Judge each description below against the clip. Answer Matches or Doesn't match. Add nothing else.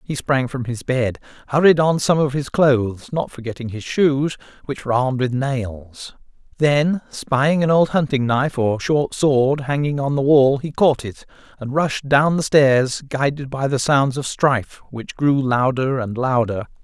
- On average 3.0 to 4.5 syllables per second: Matches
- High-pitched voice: Doesn't match